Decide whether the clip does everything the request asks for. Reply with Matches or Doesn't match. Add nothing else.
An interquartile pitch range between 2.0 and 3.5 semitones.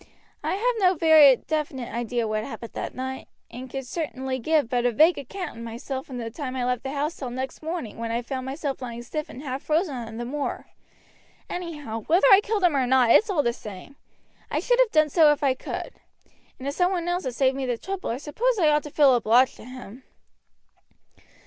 Doesn't match